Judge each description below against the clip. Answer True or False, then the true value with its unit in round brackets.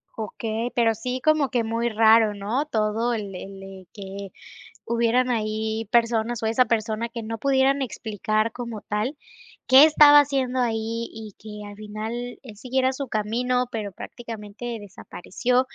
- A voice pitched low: False (225 Hz)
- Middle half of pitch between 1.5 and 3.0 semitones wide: True (2.6 semitones)